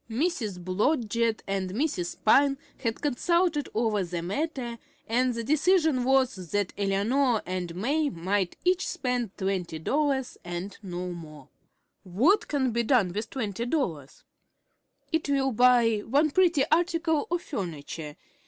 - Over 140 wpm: No, slow, 135 wpm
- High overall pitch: Yes, high, 235 Hz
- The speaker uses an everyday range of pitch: No, wide, 6.9 semitones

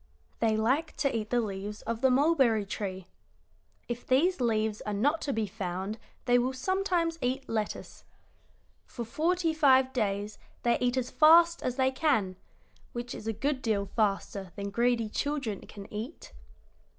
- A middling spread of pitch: Yes, average, 4.7 semitones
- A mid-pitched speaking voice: No, high, 240 Hz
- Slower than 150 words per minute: No, average, 160 wpm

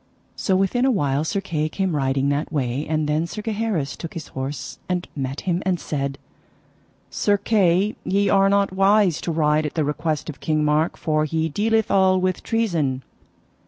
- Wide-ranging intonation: No, average, 4.6 semitones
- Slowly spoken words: No, average, 185 wpm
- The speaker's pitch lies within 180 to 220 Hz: No, medium, 165 Hz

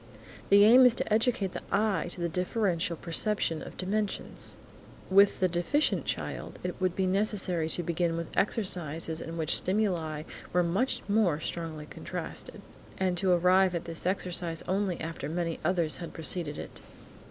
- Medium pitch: Yes, medium, 180 Hz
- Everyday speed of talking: Yes, average, 165 wpm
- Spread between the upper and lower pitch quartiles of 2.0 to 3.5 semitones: Yes, average, 3.1 semitones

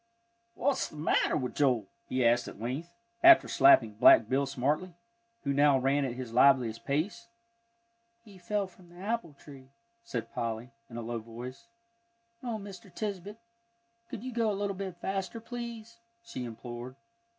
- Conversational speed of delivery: Yes, average, 160 wpm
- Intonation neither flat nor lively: No, wide, 8.7 semitones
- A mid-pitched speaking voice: Yes, medium, 155 Hz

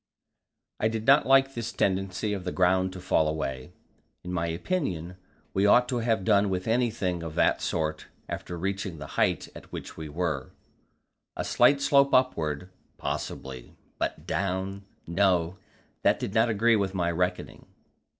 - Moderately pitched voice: No, very low, 95 Hz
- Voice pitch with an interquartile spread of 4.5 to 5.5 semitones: Yes, average, 4.8 semitones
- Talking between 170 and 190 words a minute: No, average, 160 wpm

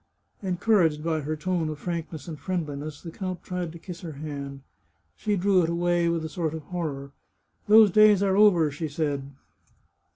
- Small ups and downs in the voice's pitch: No, average, 3.2 semitones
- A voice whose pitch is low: No, medium, 165 Hz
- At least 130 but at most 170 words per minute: No, average, 185 wpm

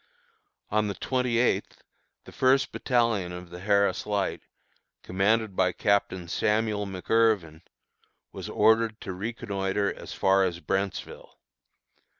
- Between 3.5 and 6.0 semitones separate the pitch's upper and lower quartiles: No, average, 3.0 semitones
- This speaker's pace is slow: Yes, slow, 120 wpm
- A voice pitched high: No, low, 100 Hz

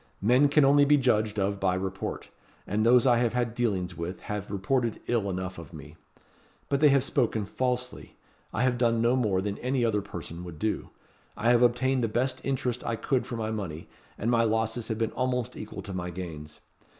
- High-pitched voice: No, low, 115 Hz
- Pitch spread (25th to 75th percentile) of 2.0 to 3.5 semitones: No, average, 4.3 semitones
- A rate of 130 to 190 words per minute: No, fast, 205 wpm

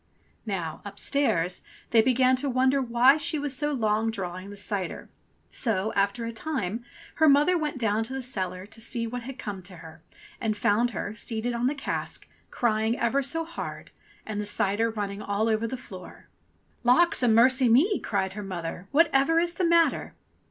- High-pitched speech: Yes, high, 230 Hz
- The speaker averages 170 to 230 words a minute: Yes, average, 180 wpm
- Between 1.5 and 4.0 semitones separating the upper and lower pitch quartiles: No, average, 4.7 semitones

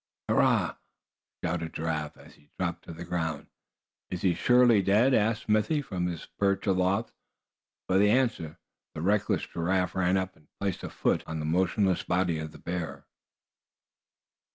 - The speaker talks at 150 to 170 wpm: Yes, average, 155 wpm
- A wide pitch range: No, average, 3.3 semitones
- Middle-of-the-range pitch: No, very low, 90 Hz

